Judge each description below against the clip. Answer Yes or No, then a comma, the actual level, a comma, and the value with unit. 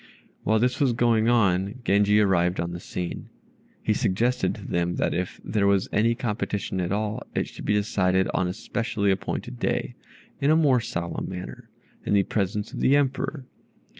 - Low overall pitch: Yes, low, 105 Hz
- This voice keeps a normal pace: Yes, average, 180 wpm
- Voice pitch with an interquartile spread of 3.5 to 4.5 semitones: Yes, average, 3.9 semitones